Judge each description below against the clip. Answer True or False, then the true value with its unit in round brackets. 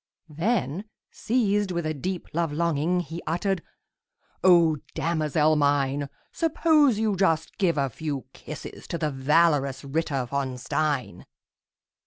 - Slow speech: True (125 wpm)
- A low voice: False (160 Hz)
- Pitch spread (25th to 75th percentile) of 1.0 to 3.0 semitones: False (4.1 semitones)